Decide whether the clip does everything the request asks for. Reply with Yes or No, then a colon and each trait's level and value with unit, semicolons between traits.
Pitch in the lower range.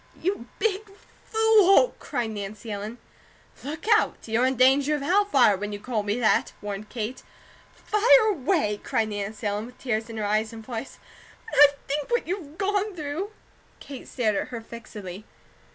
No: very high, 250 Hz